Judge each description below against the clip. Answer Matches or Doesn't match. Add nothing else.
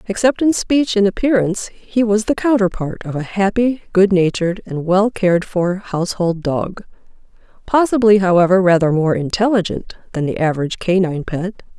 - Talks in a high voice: Matches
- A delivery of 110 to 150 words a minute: Matches